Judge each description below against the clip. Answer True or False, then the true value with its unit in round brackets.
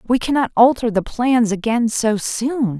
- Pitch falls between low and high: False (235 Hz)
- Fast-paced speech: False (170 wpm)